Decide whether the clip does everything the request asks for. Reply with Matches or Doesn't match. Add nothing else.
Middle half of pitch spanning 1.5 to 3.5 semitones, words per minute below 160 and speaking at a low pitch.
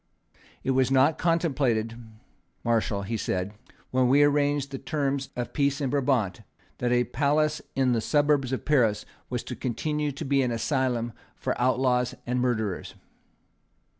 Matches